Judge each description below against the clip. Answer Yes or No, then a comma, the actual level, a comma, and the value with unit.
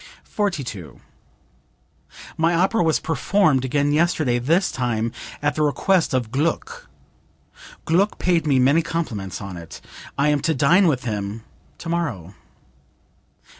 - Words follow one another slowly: Yes, slow, 125 wpm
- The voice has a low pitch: No, medium, 145 Hz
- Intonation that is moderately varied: No, wide, 5.8 semitones